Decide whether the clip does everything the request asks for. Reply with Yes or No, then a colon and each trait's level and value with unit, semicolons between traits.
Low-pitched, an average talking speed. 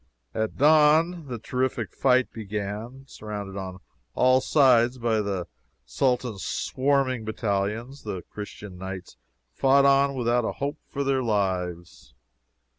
No: low, 120 Hz; slow, 120 wpm